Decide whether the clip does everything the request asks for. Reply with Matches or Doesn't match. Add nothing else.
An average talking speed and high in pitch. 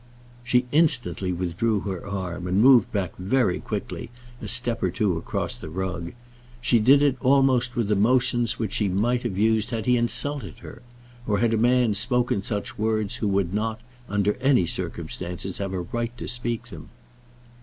Doesn't match